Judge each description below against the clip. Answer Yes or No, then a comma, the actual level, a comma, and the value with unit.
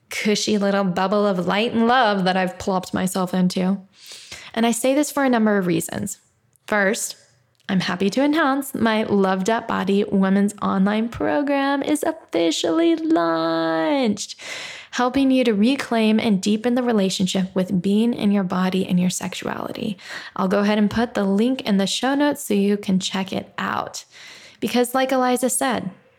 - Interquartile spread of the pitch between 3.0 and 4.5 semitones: No, average, 5.0 semitones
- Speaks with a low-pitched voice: No, high, 210 Hz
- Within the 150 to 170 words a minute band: Yes, average, 165 wpm